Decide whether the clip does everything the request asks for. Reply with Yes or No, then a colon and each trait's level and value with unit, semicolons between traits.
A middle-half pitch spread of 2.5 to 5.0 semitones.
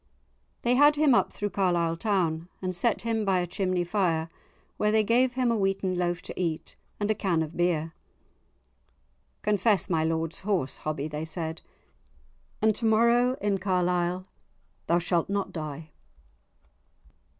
Yes: average, 4.3 semitones